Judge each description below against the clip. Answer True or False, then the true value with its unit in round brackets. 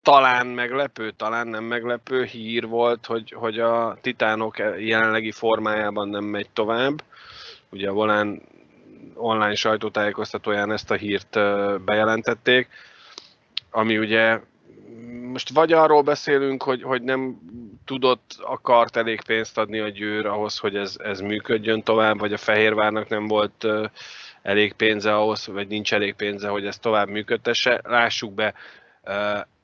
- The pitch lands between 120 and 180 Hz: False (110 Hz)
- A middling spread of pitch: False (2.1 semitones)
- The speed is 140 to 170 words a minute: False (130 wpm)